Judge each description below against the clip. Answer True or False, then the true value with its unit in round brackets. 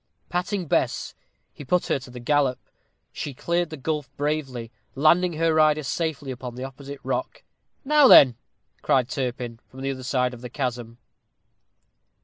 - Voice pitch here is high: False (140 Hz)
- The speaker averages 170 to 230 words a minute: False (155 wpm)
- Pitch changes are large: False (3.7 semitones)